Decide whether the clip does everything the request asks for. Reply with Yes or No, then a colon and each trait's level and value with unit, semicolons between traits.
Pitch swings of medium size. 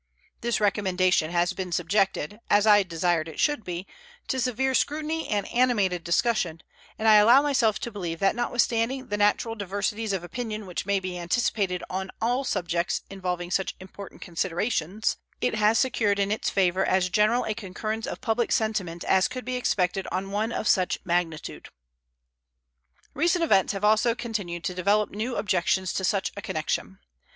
Yes: average, 3.8 semitones